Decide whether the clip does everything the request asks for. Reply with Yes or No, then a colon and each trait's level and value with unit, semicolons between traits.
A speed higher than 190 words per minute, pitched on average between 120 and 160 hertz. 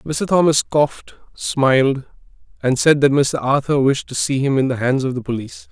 Yes: average, 200 wpm; medium, 140 Hz